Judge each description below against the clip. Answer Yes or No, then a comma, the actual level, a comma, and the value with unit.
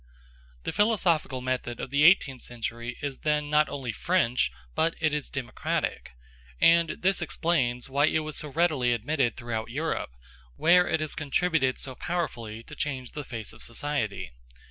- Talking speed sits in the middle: Yes, average, 160 wpm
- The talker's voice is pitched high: No, medium, 140 Hz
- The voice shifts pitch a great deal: No, average, 4.6 semitones